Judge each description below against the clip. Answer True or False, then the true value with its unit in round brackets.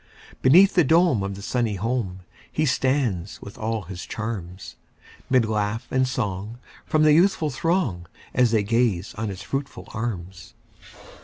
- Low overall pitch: True (115 Hz)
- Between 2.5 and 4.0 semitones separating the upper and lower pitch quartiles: False (5.1 semitones)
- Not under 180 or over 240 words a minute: False (150 wpm)